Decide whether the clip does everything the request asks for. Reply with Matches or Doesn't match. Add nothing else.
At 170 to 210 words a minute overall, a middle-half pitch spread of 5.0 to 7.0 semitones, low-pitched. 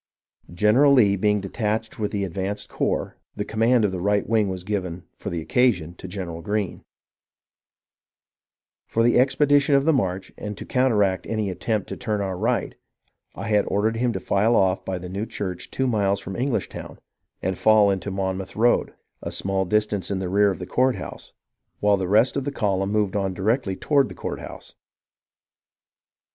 Doesn't match